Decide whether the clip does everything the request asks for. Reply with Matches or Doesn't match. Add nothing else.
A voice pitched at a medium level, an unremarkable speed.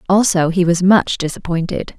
Matches